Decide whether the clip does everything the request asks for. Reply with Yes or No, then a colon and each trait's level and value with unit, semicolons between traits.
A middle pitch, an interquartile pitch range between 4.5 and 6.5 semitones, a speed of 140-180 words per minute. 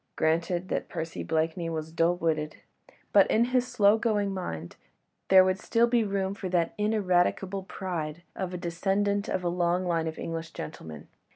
No: medium, 180 Hz; average, 3.4 semitones; average, 170 wpm